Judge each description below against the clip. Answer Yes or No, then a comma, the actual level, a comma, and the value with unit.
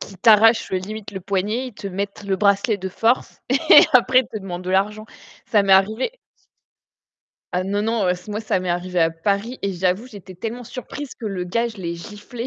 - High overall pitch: Yes, high, 200 Hz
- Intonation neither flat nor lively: Yes, average, 3.3 semitones